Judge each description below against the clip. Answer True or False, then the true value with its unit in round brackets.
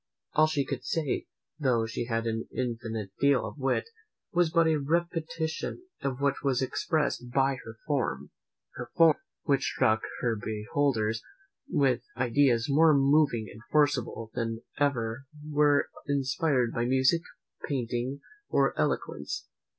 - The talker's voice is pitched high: False (135 Hz)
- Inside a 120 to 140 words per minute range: True (135 wpm)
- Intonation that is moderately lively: True (4.0 semitones)